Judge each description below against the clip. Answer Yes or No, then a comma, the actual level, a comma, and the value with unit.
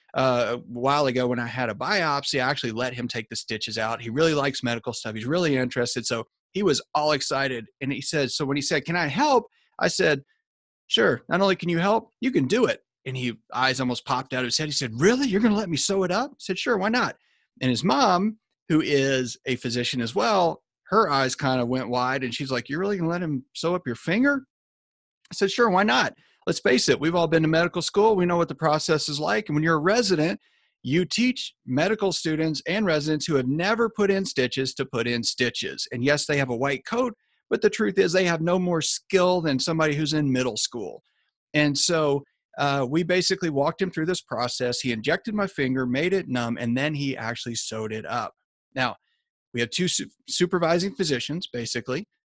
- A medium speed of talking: No, fast, 230 wpm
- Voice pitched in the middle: Yes, medium, 150 Hz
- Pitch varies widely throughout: Yes, wide, 6.3 semitones